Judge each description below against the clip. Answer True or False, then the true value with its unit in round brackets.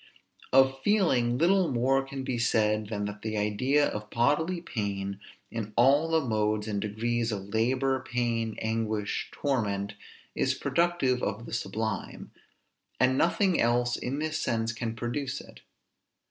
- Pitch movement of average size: True (3.9 semitones)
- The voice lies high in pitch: False (120 Hz)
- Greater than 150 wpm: False (145 wpm)